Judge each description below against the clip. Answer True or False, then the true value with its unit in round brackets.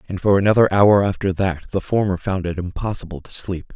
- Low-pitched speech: True (95 Hz)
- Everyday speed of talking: False (210 wpm)